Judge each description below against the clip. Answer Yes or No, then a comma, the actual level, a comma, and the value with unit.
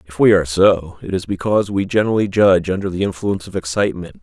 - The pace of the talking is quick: Yes, fast, 215 wpm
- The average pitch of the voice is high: No, very low, 95 Hz